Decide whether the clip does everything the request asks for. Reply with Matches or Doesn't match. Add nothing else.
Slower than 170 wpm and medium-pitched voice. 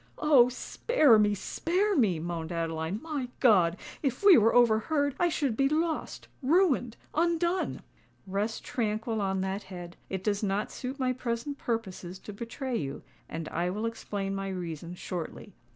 Doesn't match